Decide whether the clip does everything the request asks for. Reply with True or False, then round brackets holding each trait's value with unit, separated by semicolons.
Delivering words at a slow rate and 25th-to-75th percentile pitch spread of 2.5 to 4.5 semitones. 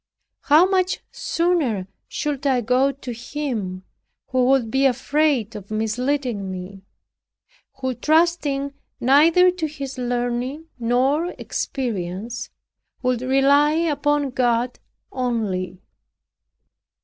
True (100 wpm; 3.8 semitones)